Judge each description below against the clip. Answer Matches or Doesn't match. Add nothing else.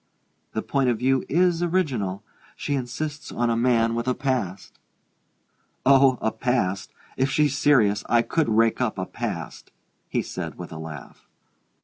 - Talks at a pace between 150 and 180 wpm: Matches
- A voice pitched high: Doesn't match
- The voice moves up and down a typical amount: Matches